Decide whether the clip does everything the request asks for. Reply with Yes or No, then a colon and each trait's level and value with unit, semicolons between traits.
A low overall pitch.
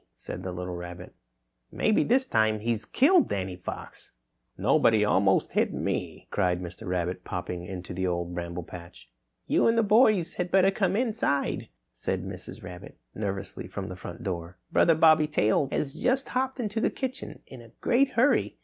Yes: low, 110 Hz